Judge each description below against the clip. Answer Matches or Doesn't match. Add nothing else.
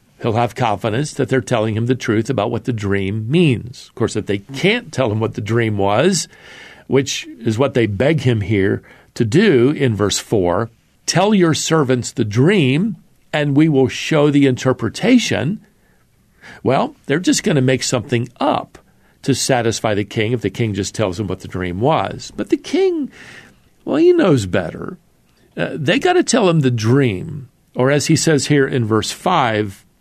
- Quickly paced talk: Doesn't match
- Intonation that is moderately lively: Doesn't match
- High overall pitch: Doesn't match